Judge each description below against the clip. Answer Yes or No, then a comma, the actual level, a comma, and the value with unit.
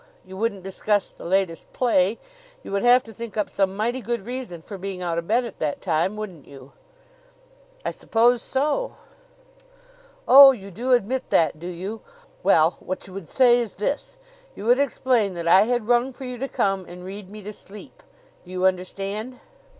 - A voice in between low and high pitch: No, high, 205 Hz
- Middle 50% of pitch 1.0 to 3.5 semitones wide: No, average, 4.7 semitones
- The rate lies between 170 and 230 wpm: Yes, average, 190 wpm